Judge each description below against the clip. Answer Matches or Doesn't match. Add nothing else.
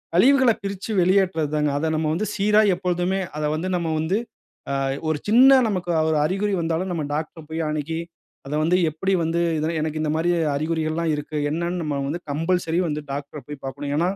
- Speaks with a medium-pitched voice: Matches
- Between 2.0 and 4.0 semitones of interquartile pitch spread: Matches